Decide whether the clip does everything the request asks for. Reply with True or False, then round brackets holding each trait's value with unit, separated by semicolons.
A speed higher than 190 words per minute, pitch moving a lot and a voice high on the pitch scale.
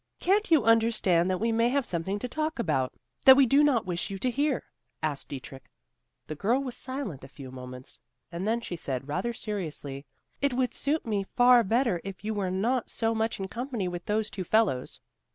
True (205 wpm; 6.2 semitones; 215 Hz)